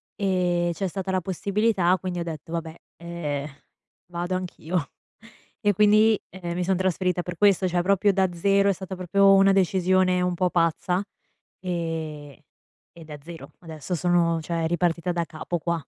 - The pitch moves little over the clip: Yes, narrow, 2.0 semitones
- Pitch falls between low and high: Yes, medium, 180 Hz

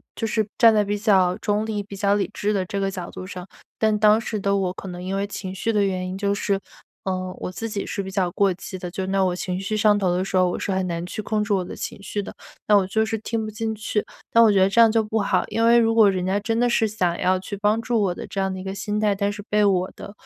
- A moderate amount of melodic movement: No, narrow, 2.3 semitones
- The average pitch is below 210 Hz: Yes, high, 200 Hz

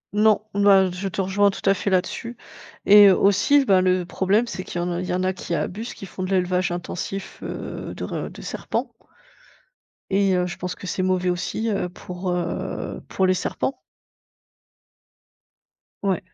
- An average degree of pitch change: No, narrow, 1.8 semitones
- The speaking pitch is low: No, medium, 185 Hz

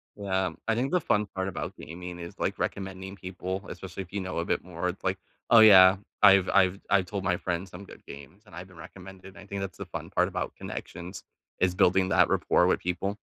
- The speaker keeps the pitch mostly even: Yes, narrow, 1.5 semitones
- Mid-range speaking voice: No, very low, 95 Hz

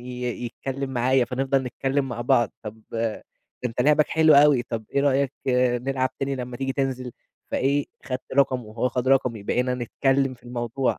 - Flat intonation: Yes, narrow, 2.0 semitones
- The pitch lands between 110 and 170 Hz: Yes, low, 130 Hz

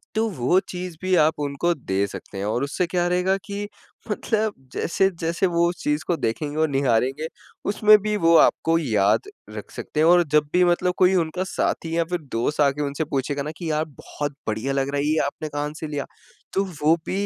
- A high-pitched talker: No, medium, 155 Hz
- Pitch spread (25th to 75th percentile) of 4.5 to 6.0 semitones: No, average, 4.1 semitones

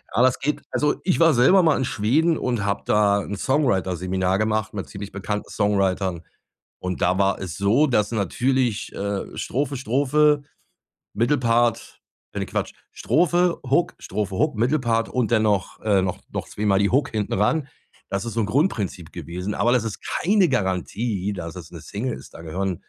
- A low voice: Yes, low, 110 Hz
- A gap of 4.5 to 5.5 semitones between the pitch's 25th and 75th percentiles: Yes, average, 5.1 semitones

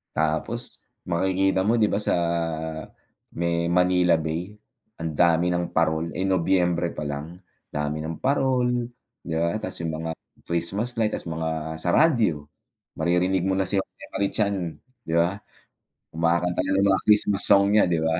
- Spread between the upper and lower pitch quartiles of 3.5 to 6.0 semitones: No, average, 3.1 semitones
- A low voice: Yes, very low, 90 Hz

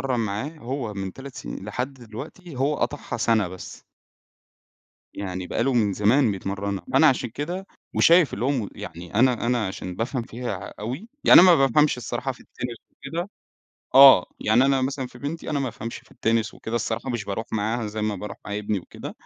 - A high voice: No, low, 120 Hz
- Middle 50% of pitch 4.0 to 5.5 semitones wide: Yes, average, 4.5 semitones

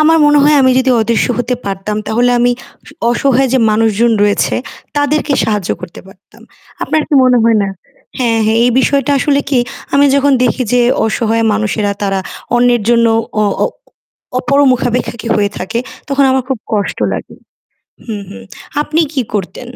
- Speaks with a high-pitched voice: Yes, high, 240 Hz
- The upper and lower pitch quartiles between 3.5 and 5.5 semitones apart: Yes, average, 3.9 semitones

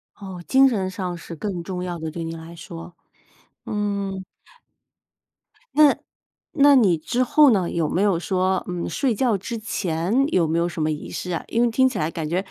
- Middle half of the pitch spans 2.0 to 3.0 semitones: No, average, 4.5 semitones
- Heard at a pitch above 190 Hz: No, medium, 185 Hz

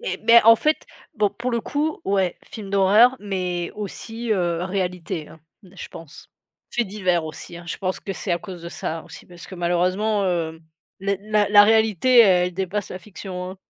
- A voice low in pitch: No, high, 195 Hz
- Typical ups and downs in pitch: Yes, average, 3.1 semitones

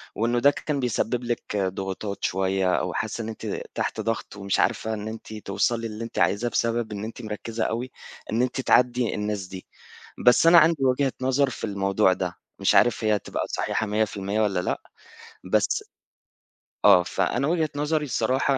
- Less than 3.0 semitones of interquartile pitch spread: No, average, 3.8 semitones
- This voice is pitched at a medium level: No, low, 110 Hz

